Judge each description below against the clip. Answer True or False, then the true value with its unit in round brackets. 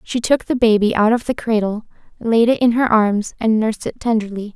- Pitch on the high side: True (225 Hz)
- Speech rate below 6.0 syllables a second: True (5.4 syllables/s)